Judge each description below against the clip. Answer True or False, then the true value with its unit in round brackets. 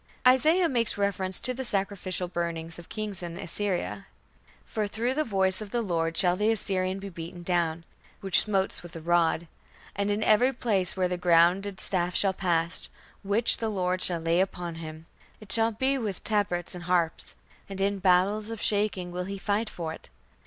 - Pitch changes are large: False (3.3 semitones)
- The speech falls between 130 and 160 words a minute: False (185 wpm)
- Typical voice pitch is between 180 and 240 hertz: True (190 Hz)